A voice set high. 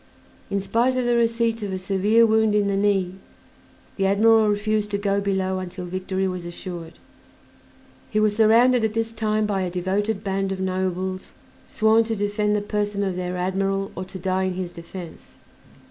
Yes: high, 200 Hz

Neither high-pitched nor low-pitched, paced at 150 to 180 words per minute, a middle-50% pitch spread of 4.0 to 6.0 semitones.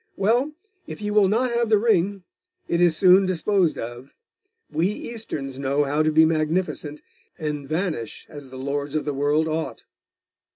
Yes: medium, 160 Hz; average, 165 wpm; average, 5.3 semitones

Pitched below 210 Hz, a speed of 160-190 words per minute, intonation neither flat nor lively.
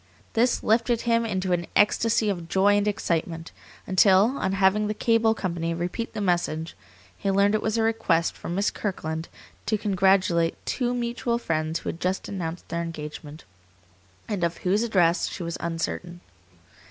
Yes: high, 190 Hz; average, 165 wpm; average, 4.2 semitones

